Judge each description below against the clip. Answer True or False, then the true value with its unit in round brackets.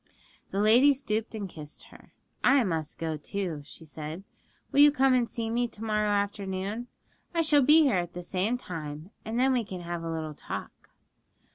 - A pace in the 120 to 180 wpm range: False (190 wpm)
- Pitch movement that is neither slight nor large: False (6.3 semitones)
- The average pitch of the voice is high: True (205 Hz)